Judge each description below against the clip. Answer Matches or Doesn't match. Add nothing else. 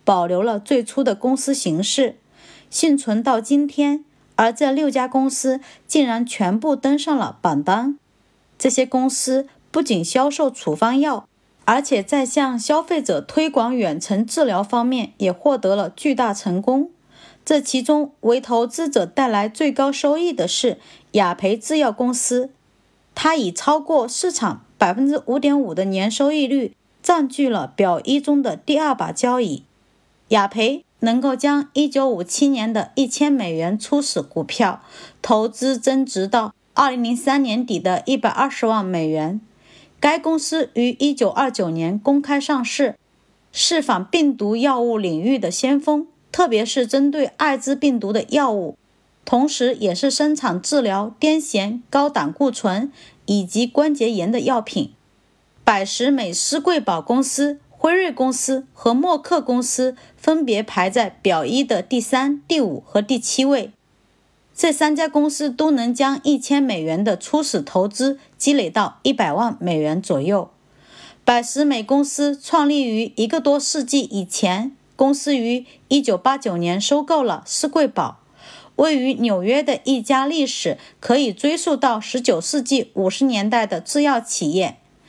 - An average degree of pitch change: Matches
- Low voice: Doesn't match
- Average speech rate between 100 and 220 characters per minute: Matches